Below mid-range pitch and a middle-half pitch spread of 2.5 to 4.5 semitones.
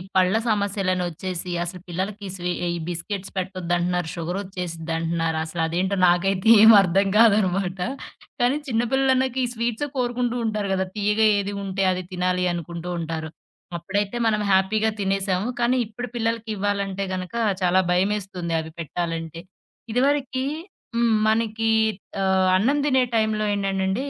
No: high, 195 Hz; average, 3.7 semitones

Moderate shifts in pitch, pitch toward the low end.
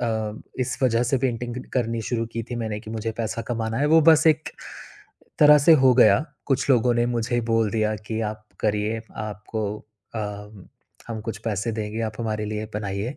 No: narrow, 2.1 semitones; low, 115 Hz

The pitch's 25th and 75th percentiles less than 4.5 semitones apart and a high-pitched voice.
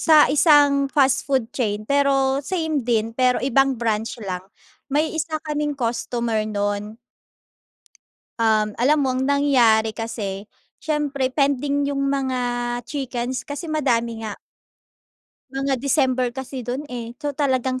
Yes: average, 3.6 semitones; very high, 260 Hz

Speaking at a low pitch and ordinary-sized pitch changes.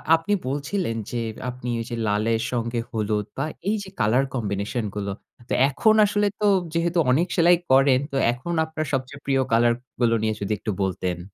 No: low, 125 Hz; wide, 6.2 semitones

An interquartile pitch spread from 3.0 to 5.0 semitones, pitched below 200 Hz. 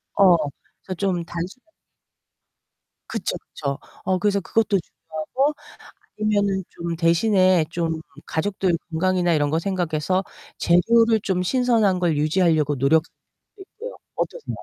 Yes: average, 3.8 semitones; medium, 185 Hz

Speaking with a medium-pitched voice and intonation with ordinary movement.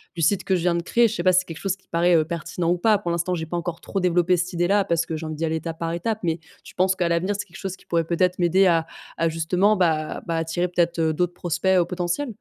No: medium, 175 Hz; narrow, 1.9 semitones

